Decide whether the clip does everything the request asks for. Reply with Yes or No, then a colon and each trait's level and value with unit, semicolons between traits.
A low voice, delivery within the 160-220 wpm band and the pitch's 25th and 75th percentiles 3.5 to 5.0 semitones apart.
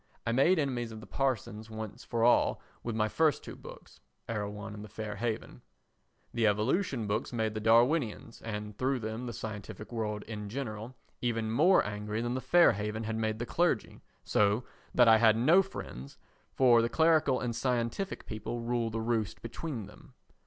No: low, 115 Hz; average, 180 wpm; average, 2.7 semitones